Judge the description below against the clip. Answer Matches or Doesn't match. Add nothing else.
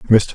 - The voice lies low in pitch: Matches